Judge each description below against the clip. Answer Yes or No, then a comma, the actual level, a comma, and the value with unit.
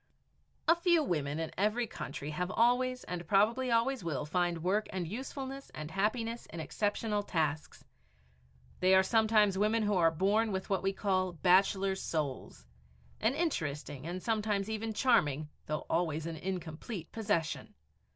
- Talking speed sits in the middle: Yes, average, 150 wpm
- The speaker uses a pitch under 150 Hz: No, high, 195 Hz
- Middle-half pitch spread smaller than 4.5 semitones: No, average, 5.3 semitones